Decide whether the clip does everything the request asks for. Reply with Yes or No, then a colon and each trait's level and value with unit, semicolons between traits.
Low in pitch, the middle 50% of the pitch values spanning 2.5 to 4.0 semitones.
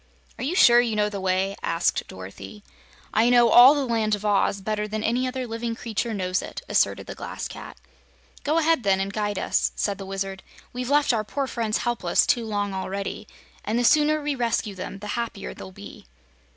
No: high, 215 Hz; average, 3.7 semitones